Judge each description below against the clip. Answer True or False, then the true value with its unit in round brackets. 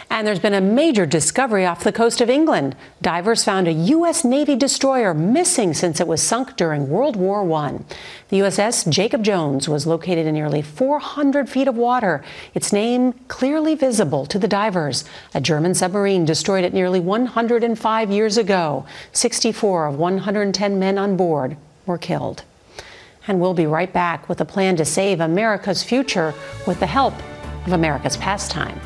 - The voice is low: False (190 Hz)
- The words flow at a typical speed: True (165 wpm)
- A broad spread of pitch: True (6.1 semitones)